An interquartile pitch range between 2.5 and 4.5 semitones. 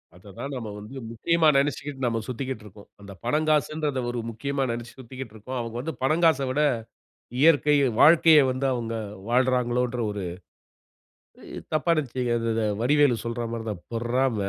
Yes: average, 3.9 semitones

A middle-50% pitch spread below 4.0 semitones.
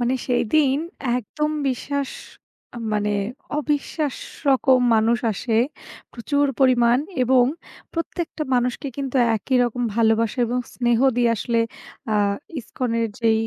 Yes: average, 2.9 semitones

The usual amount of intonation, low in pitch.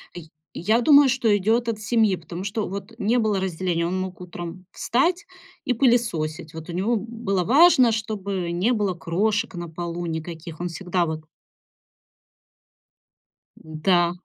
No: average, 4.7 semitones; high, 190 Hz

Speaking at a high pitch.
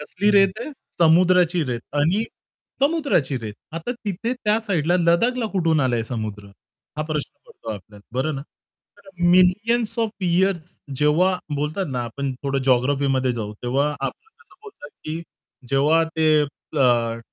No: medium, 160 Hz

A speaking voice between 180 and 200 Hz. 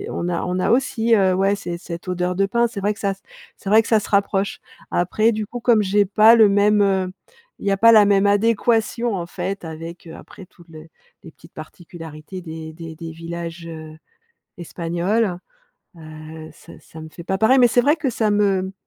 Yes: high, 190 Hz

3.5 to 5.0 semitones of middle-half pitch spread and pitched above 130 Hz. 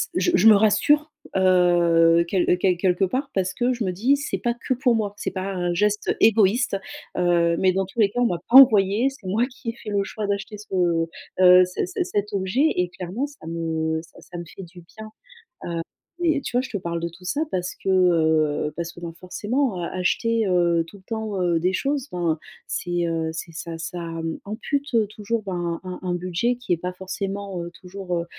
Yes: average, 4.1 semitones; medium, 185 Hz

